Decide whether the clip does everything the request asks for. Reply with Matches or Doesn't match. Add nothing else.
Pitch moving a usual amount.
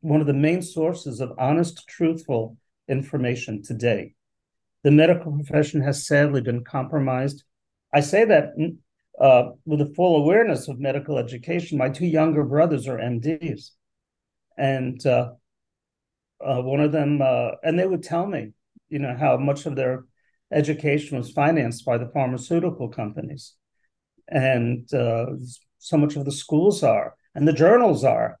Matches